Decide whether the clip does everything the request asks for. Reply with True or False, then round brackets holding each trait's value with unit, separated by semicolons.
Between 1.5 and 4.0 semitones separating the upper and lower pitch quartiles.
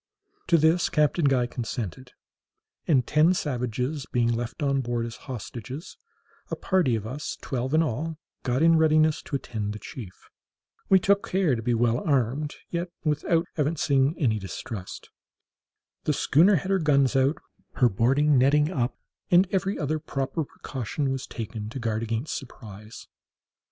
False (4.7 semitones)